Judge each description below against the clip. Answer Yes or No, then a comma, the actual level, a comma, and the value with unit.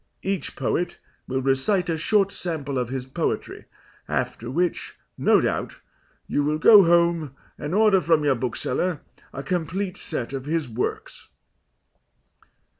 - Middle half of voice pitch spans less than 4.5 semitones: No, average, 5.1 semitones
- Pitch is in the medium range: Yes, medium, 160 Hz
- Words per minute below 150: Yes, slow, 135 wpm